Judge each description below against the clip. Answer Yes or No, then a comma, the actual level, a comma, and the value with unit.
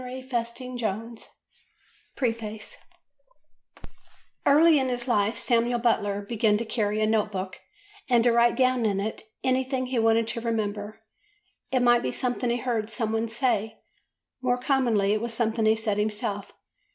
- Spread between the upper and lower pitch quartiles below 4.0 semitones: Yes, narrow, 2.4 semitones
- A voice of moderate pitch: No, high, 230 Hz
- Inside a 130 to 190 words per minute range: Yes, average, 150 wpm